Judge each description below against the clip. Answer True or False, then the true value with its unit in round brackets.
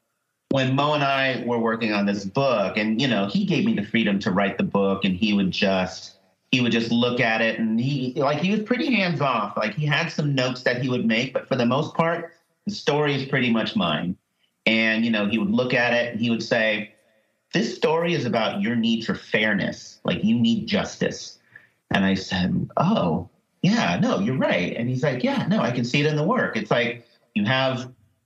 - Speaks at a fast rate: True (225 wpm)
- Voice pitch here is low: True (130 Hz)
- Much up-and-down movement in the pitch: True (6.8 semitones)